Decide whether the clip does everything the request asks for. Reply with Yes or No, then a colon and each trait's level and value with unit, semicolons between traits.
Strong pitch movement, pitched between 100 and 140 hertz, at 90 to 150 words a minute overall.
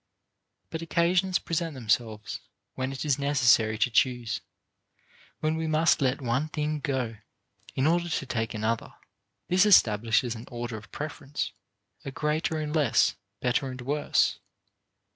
No: average, 4.7 semitones; low, 135 Hz; average, 140 wpm